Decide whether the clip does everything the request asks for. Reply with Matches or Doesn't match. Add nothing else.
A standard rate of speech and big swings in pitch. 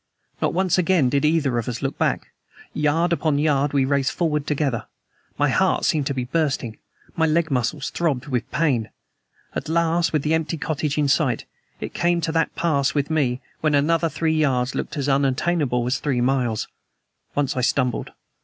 Doesn't match